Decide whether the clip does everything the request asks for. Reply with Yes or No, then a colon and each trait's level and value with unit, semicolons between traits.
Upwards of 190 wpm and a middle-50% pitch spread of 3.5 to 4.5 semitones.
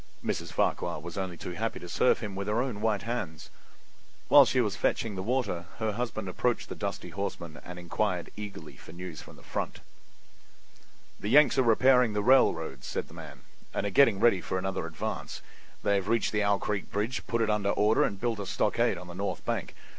Yes: fast, 205 wpm; average, 3.9 semitones